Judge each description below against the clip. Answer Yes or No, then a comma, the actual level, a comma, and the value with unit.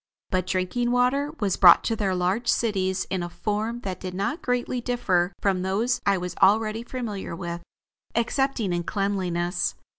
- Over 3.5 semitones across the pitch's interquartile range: Yes, average, 4.5 semitones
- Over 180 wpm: No, average, 160 wpm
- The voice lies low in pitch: No, high, 200 Hz